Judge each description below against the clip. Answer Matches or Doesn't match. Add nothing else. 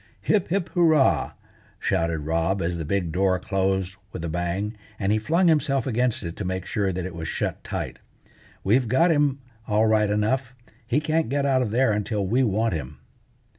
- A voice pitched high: Doesn't match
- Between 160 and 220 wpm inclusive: Matches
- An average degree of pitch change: Doesn't match